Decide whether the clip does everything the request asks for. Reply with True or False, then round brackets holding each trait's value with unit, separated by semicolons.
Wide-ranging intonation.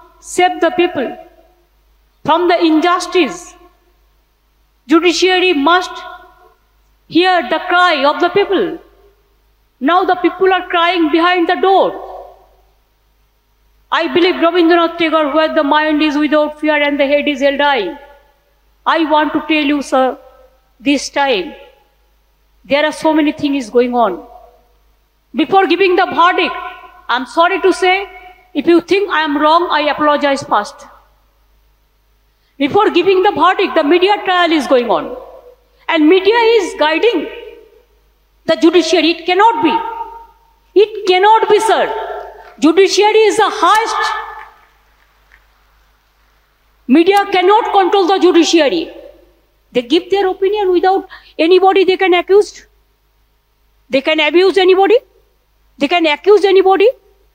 False (3.8 semitones)